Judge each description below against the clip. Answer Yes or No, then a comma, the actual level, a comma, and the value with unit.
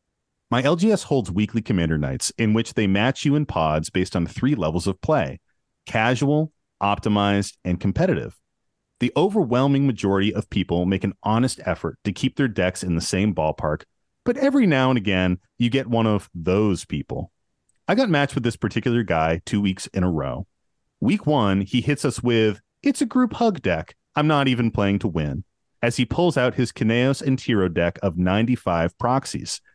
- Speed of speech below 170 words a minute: No, average, 185 wpm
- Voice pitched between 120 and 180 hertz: No, low, 110 Hz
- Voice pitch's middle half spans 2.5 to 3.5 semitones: No, wide, 5.6 semitones